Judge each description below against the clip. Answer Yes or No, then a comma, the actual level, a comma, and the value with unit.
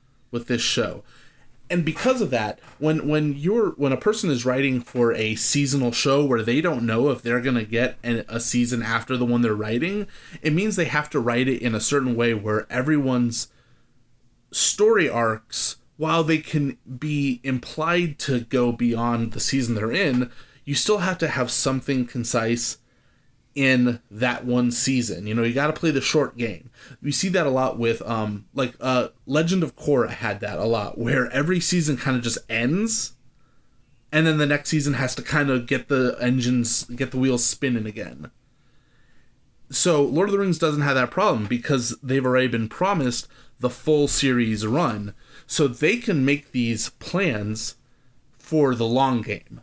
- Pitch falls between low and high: No, low, 130 Hz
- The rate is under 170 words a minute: No, average, 185 wpm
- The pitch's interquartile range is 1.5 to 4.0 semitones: Yes, average, 3.5 semitones